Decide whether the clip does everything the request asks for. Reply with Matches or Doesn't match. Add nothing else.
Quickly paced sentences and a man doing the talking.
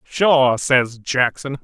Doesn't match